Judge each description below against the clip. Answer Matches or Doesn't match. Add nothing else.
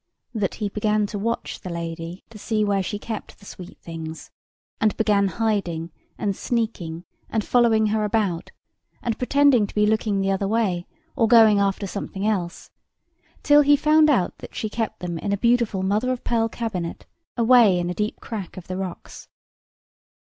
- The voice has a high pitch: Matches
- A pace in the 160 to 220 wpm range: Matches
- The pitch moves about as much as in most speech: Matches